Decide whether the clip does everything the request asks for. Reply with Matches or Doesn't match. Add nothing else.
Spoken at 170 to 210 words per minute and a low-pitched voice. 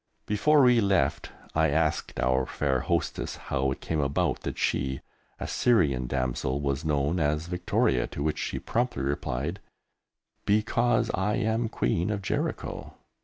Doesn't match